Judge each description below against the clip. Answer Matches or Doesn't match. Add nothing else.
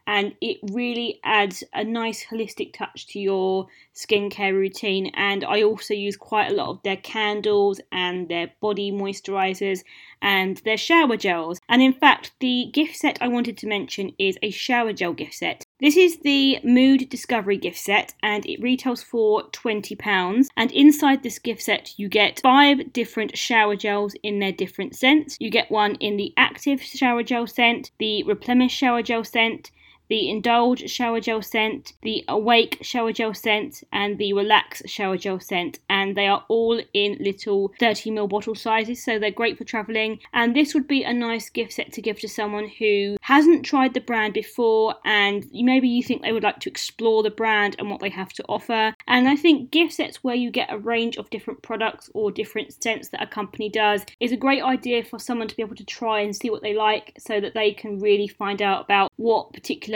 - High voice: Matches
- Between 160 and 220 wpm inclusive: Matches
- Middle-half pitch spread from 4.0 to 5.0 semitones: Doesn't match